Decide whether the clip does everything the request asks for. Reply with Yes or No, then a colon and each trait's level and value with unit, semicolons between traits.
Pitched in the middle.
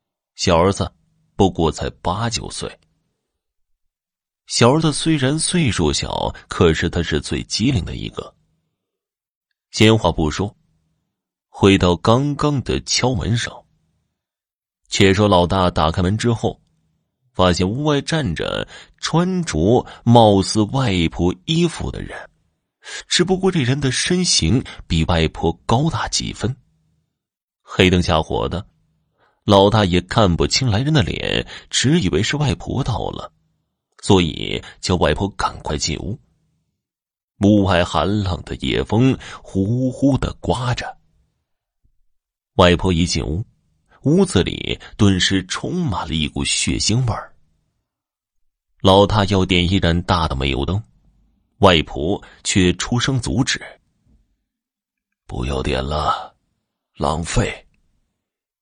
No: low, 100 Hz